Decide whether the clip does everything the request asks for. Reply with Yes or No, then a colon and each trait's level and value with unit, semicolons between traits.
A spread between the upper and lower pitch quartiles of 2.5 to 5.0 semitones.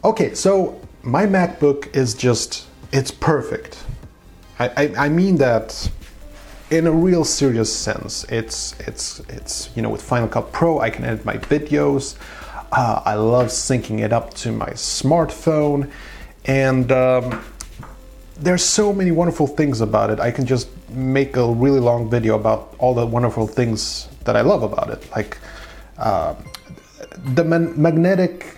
No: wide, 5.6 semitones